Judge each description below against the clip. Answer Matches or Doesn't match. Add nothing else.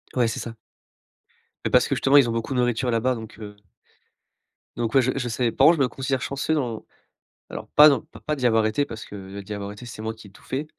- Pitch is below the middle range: Matches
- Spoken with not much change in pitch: Doesn't match